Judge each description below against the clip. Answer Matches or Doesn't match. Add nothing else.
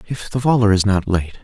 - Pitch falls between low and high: Doesn't match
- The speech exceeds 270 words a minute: Doesn't match